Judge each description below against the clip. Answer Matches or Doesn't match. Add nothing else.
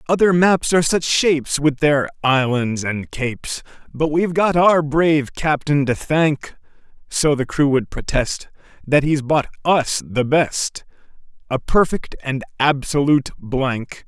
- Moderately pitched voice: Matches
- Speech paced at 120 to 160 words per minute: Matches